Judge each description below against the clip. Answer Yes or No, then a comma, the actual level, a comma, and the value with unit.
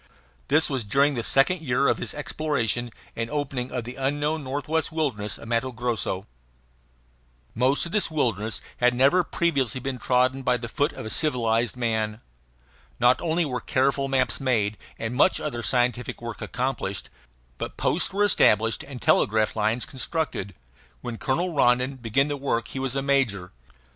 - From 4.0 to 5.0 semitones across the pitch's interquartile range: No, average, 3.4 semitones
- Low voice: Yes, low, 130 Hz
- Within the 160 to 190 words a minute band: Yes, average, 165 wpm